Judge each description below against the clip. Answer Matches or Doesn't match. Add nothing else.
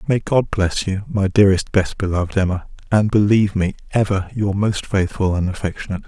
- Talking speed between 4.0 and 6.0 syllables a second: Matches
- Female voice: Doesn't match